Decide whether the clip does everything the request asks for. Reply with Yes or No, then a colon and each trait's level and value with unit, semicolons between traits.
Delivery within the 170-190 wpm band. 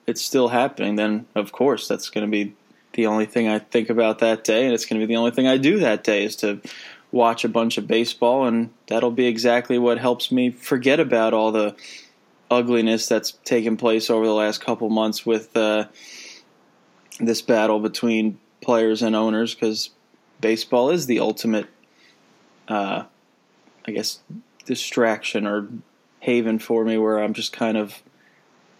Yes: average, 175 wpm